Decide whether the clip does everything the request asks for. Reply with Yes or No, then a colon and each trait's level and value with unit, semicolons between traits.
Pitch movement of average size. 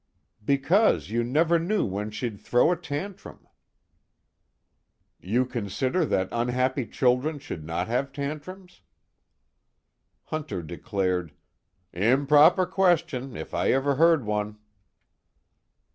No: wide, 6.8 semitones